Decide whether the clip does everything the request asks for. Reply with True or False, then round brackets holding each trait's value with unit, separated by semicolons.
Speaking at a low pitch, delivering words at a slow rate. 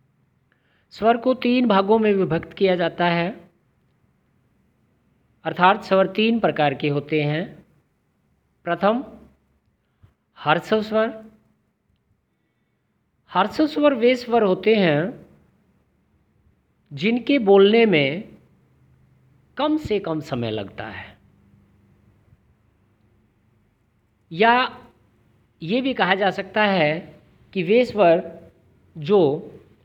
False (175 Hz; 85 wpm)